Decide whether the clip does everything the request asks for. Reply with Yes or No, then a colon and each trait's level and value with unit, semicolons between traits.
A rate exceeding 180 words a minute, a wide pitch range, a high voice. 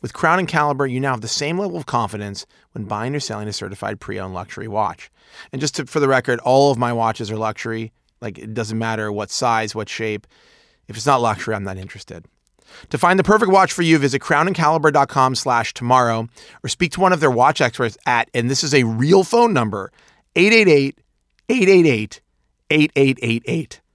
No: average, 190 wpm; wide, 5.7 semitones; low, 125 Hz